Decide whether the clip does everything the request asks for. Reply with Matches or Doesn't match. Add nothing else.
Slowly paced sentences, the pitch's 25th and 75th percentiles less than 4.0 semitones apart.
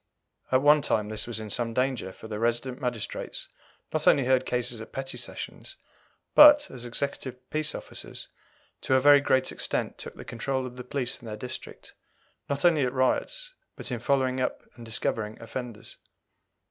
Doesn't match